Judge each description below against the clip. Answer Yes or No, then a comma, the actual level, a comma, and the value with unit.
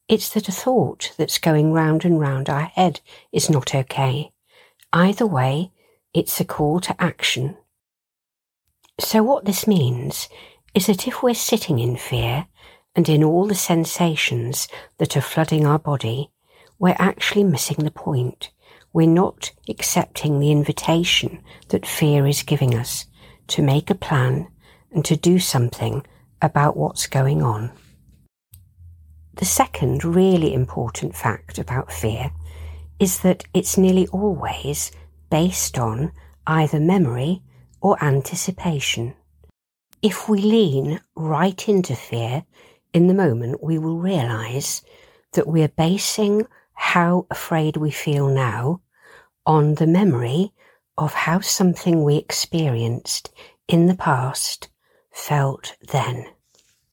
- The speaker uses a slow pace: Yes, slow, 130 wpm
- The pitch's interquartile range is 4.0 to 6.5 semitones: Yes, wide, 5.4 semitones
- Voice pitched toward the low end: No, medium, 155 Hz